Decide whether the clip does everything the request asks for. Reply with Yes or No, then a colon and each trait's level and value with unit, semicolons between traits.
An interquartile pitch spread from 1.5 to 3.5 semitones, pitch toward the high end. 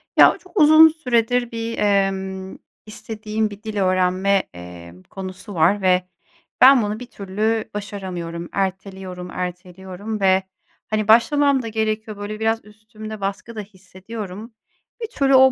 Yes: average, 3.0 semitones; high, 205 Hz